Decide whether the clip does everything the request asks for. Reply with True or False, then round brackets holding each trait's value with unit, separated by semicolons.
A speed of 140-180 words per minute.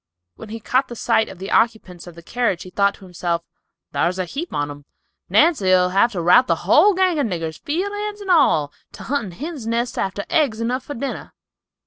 False (205 wpm)